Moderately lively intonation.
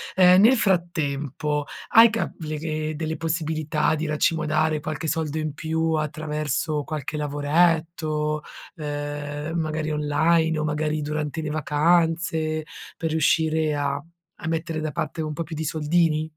No: narrow, 1.3 semitones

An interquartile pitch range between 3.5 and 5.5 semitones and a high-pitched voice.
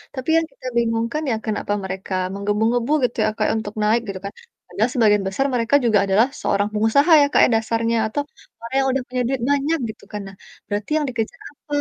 Yes: average, 3.8 semitones; high, 230 Hz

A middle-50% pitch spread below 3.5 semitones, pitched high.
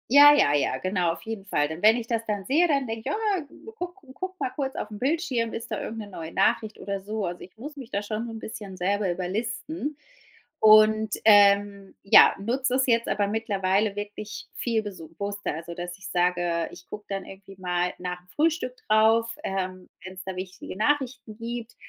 No: average, 3.9 semitones; high, 210 Hz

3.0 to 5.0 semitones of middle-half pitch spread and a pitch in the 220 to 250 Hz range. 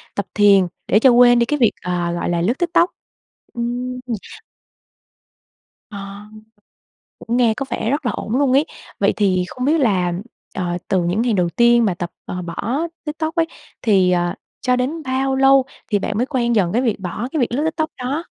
No: wide, 5.4 semitones; high, 235 Hz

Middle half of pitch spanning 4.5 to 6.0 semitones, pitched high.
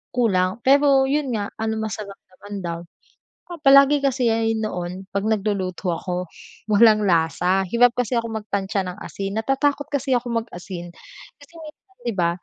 Yes: average, 5.0 semitones; high, 220 Hz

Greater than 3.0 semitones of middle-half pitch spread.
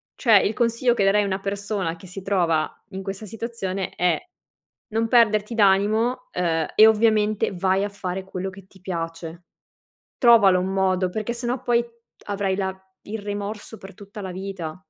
No: narrow, 2.6 semitones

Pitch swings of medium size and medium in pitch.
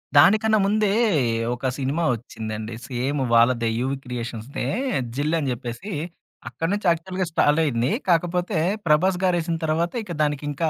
No: wide, 5.9 semitones; medium, 150 Hz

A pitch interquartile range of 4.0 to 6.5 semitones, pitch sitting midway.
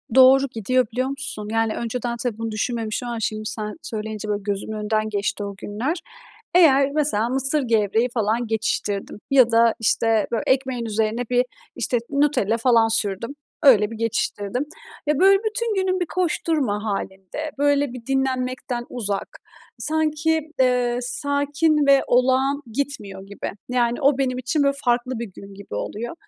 No: average, 4.3 semitones; high, 245 Hz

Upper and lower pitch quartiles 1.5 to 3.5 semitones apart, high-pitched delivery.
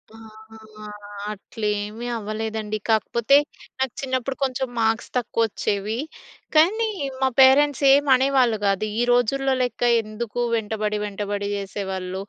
No: average, 3.9 semitones; high, 225 Hz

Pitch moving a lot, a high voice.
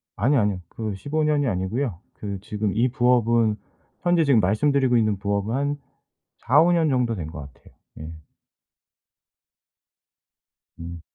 No: wide, 5.7 semitones; low, 115 Hz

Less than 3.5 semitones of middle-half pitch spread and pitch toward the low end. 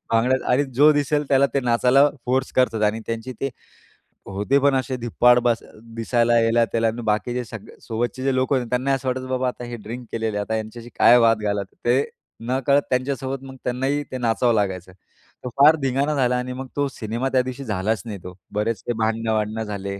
Yes: average, 2.9 semitones; low, 120 Hz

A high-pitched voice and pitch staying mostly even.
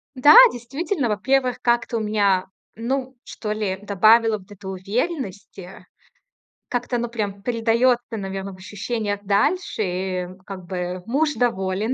No: high, 215 Hz; average, 4.0 semitones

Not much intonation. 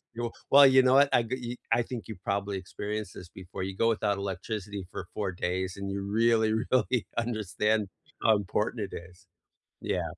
No: average, 3.0 semitones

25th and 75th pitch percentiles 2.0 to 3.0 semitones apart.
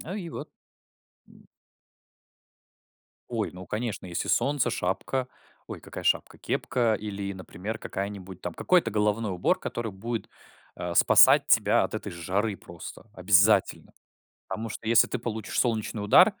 No: average, 3.4 semitones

